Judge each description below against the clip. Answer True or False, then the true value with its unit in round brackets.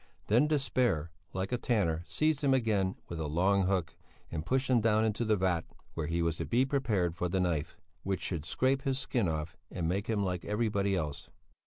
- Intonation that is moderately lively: False (5.9 semitones)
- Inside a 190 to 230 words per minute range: True (205 wpm)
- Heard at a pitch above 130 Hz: False (100 Hz)